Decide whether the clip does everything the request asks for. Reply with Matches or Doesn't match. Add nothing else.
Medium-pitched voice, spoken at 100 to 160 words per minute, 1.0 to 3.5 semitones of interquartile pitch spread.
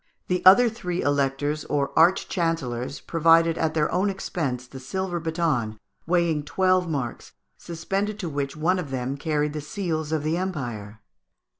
Doesn't match